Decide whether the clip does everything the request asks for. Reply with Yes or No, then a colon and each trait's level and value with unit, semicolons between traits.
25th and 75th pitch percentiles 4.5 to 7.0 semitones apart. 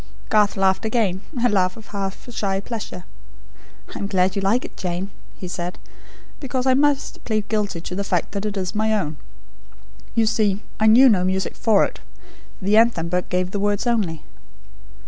No: average, 2.9 semitones